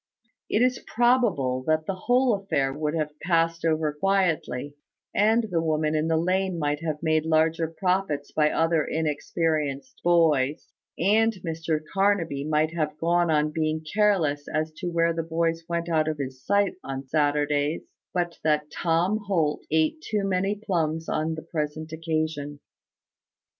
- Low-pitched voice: No, medium, 160 Hz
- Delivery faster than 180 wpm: No, average, 155 wpm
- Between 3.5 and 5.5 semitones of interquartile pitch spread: No, average, 2.8 semitones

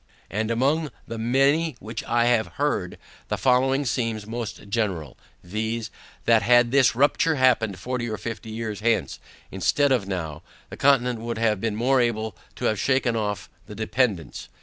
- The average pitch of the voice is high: No, low, 115 Hz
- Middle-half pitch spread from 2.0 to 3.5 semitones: Yes, average, 2.9 semitones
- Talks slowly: No, average, 165 wpm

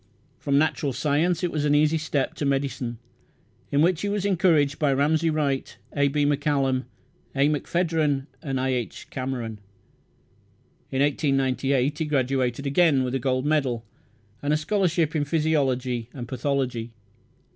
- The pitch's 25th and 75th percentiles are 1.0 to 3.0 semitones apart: Yes, narrow, 2.6 semitones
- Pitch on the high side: No, medium, 140 Hz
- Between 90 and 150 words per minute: Yes, average, 145 wpm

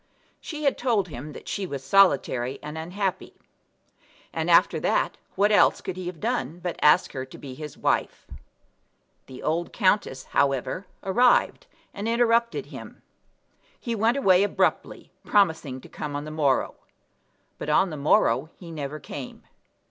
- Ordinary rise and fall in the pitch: No, wide, 6.1 semitones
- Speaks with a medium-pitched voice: Yes, medium, 165 Hz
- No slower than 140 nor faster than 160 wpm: Yes, average, 155 wpm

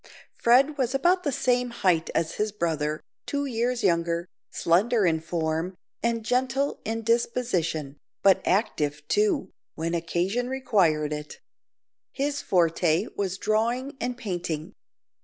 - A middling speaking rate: No, slow, 125 wpm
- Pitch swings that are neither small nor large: No, wide, 6.7 semitones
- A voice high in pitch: Yes, high, 205 Hz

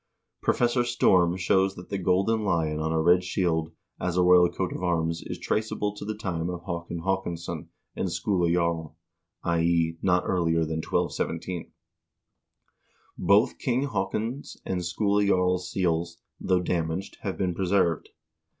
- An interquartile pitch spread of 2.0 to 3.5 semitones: Yes, narrow, 2.4 semitones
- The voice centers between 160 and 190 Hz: No, very low, 90 Hz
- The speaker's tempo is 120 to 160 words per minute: Yes, average, 150 wpm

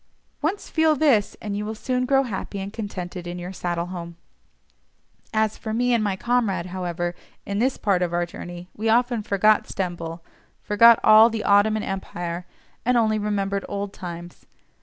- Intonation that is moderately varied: Yes, average, 4.0 semitones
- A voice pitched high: Yes, high, 205 Hz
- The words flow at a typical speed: Yes, average, 170 wpm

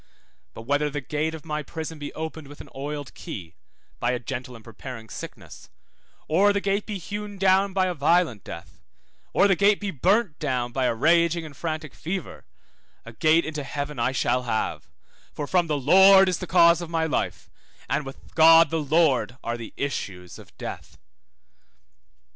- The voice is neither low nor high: Yes, medium, 155 Hz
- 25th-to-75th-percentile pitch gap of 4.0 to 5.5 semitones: Yes, average, 4.9 semitones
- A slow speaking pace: No, average, 185 wpm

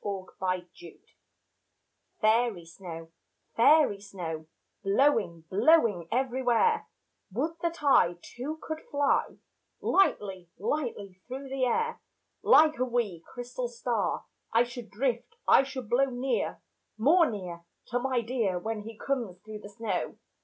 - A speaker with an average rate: No, slow, 125 wpm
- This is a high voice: Yes, high, 235 Hz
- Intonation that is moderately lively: No, wide, 5.7 semitones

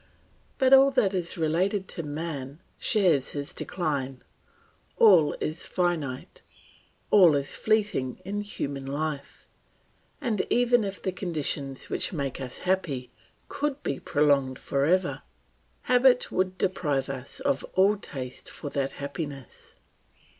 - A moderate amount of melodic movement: No, wide, 6.1 semitones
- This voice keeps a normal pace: No, slow, 125 wpm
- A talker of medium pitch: Yes, medium, 165 Hz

